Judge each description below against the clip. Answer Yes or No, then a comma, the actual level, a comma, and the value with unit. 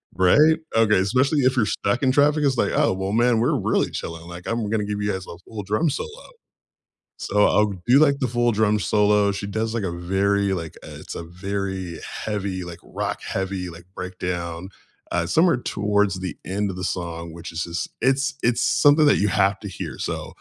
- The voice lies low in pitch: Yes, low, 100 Hz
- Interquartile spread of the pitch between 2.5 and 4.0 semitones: No, average, 4.5 semitones